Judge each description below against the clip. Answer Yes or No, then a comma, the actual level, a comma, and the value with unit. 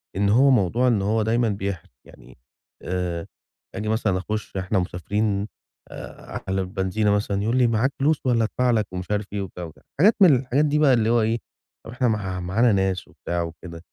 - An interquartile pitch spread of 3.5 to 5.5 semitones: Yes, average, 4.1 semitones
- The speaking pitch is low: Yes, low, 105 Hz